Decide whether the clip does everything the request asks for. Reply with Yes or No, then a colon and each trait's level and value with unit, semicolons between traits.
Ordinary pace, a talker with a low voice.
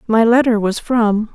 No: average, 180 wpm; high, 225 Hz